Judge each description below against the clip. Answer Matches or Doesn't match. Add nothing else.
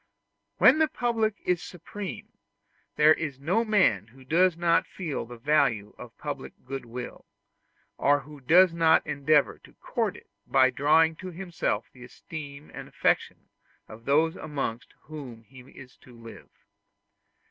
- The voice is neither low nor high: Matches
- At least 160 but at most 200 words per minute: Doesn't match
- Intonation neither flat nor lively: Matches